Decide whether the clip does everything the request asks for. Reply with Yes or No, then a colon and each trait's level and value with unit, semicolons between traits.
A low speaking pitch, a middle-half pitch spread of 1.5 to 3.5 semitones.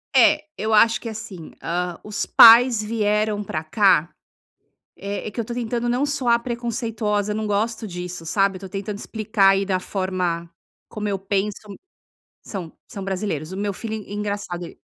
No: high, 205 Hz; average, 2.8 semitones